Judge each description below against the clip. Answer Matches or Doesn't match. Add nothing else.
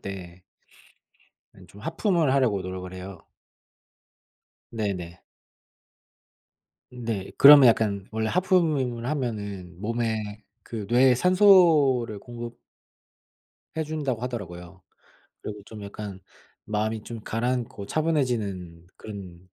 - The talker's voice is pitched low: Matches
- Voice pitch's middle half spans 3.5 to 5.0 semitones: Matches